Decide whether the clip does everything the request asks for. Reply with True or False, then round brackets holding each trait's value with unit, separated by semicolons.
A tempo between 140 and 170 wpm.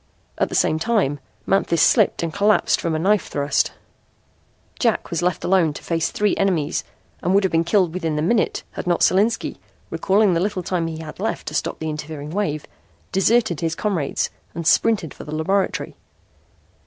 False (180 wpm)